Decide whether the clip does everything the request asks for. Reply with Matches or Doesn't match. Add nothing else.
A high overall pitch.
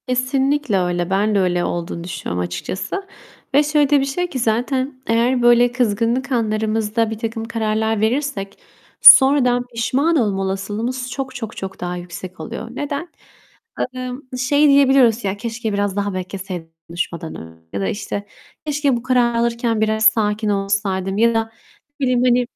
Matches